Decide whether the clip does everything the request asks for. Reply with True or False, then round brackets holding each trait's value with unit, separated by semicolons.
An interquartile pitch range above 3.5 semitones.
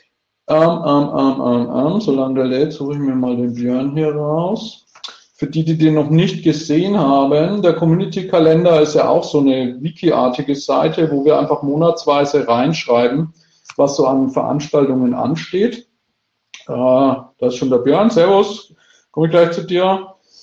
True (3.9 semitones)